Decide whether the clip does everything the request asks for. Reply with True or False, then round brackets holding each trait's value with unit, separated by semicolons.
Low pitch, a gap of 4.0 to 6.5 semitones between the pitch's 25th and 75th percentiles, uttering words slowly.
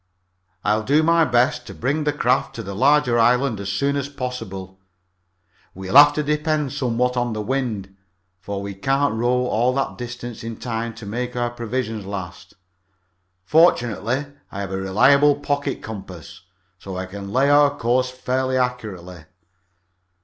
False (120 Hz; 5.2 semitones; 155 wpm)